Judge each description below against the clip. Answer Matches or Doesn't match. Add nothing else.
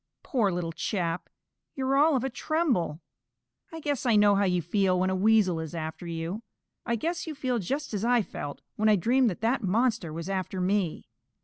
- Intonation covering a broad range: Matches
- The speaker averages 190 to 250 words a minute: Matches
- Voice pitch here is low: Doesn't match